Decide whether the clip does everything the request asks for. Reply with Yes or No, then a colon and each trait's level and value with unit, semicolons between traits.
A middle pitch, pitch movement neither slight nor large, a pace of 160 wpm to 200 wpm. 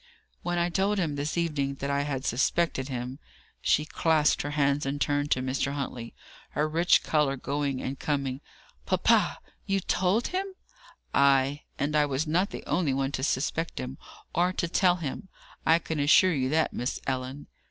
Yes: medium, 145 Hz; average, 3.6 semitones; average, 180 wpm